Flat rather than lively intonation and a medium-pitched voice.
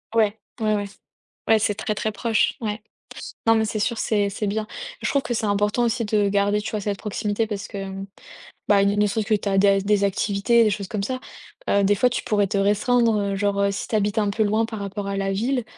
No: narrow, 1.7 semitones; high, 210 Hz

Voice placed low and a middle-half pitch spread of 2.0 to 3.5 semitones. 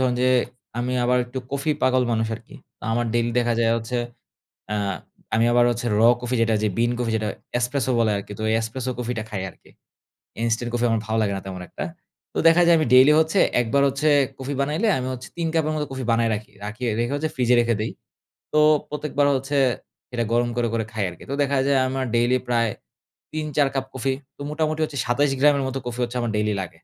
Yes: low, 125 Hz; average, 3.2 semitones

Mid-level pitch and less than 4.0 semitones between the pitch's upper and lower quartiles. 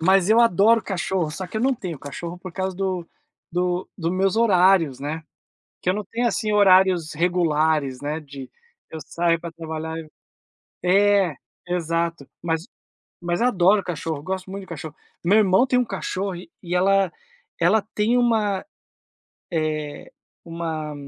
Yes: medium, 180 Hz; average, 3.3 semitones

